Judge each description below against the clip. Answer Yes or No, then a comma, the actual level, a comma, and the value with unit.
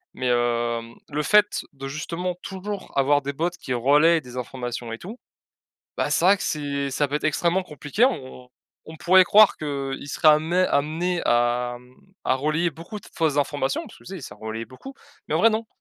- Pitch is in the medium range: Yes, medium, 145 Hz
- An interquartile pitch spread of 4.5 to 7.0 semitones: Yes, wide, 5.5 semitones